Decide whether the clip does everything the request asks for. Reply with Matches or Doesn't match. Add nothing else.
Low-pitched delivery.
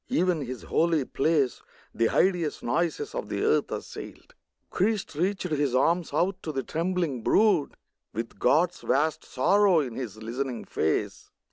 Doesn't match